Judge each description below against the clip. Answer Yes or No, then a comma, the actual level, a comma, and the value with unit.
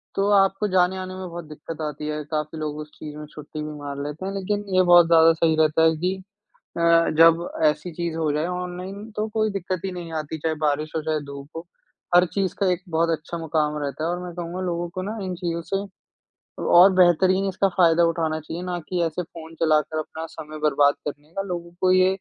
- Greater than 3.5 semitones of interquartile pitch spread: No, average, 3.0 semitones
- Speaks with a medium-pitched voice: Yes, medium, 170 Hz